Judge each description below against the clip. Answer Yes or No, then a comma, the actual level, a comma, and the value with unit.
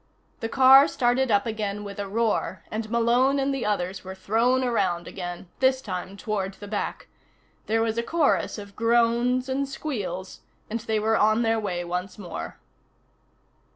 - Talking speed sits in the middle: Yes, average, 165 wpm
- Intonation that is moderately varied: Yes, average, 3.7 semitones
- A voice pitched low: No, high, 220 Hz